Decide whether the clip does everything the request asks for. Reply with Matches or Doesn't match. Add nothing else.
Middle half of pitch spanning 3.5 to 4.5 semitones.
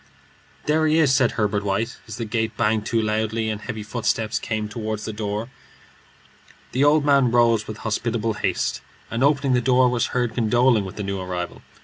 Doesn't match